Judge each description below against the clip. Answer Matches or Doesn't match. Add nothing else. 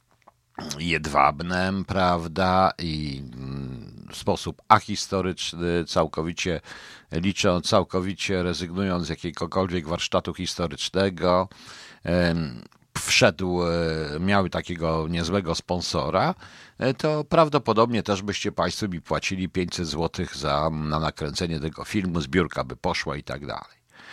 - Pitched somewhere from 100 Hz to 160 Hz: Doesn't match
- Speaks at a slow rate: Matches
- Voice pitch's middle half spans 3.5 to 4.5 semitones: Doesn't match